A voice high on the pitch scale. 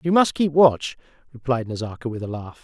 No: low, 130 Hz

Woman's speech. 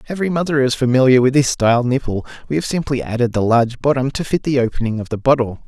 No: male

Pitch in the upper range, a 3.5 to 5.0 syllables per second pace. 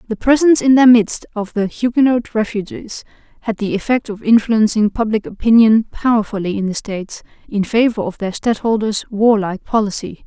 No: high, 220 Hz; 5.4 syllables/s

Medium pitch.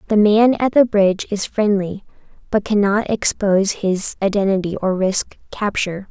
No: high, 205 Hz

